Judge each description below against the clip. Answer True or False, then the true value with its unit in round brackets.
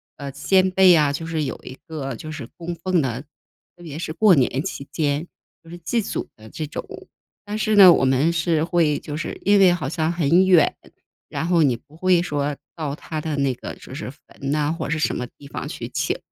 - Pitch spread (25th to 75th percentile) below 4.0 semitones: True (3.5 semitones)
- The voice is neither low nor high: True (160 Hz)